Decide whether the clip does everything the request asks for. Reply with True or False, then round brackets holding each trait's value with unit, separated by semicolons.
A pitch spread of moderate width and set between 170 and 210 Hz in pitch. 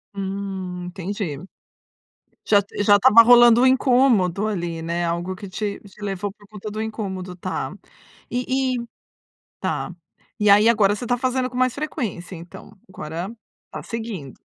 True (4.1 semitones; 205 Hz)